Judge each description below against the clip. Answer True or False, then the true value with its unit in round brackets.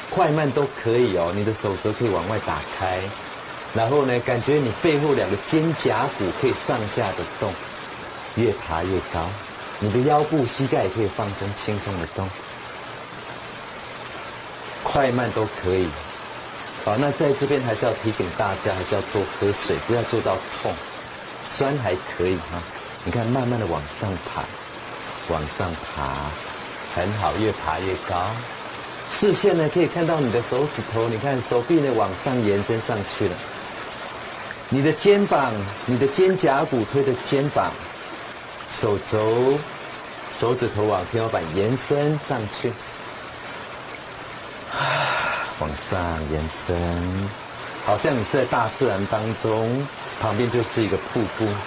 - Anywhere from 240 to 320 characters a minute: False (205 characters per minute)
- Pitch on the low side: True (115 Hz)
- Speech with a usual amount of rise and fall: False (5.7 semitones)